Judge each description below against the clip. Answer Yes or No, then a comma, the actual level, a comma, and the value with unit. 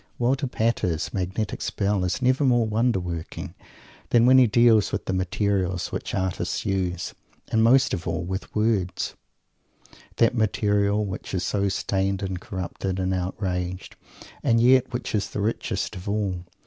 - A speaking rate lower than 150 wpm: No, average, 155 wpm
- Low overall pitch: Yes, low, 100 Hz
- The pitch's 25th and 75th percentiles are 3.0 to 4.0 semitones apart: Yes, average, 3.7 semitones